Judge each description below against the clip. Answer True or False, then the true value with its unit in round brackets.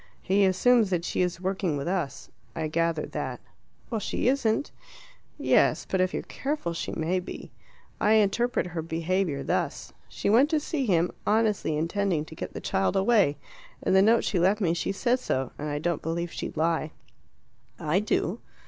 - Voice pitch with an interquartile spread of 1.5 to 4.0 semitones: False (4.4 semitones)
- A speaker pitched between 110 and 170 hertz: False (185 Hz)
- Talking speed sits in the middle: True (180 wpm)